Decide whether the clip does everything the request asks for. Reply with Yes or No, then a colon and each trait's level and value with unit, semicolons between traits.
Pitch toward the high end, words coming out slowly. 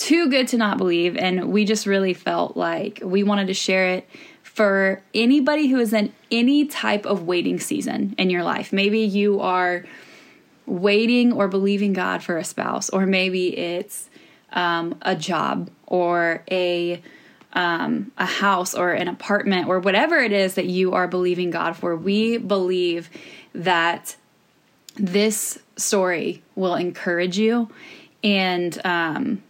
No: high, 195 Hz; average, 150 wpm